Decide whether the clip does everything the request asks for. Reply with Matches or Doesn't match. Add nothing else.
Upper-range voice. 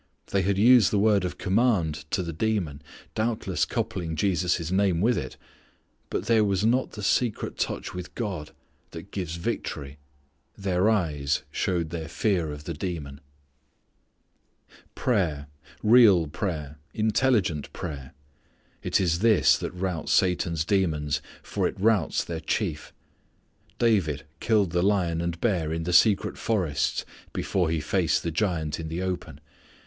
Doesn't match